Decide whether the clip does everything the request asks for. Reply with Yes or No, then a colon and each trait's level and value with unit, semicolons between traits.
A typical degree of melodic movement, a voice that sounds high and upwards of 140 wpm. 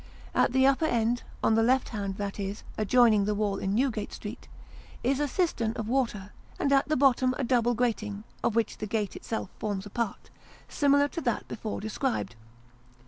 Yes: average, 3.9 semitones; high, 230 Hz; average, 190 wpm